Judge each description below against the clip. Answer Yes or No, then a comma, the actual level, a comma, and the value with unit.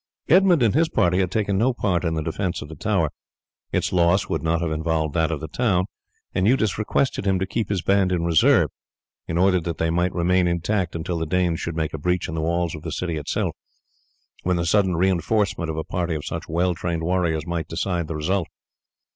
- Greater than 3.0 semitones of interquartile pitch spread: No, average, 2.7 semitones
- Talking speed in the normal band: No, fast, 220 wpm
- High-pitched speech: No, very low, 85 Hz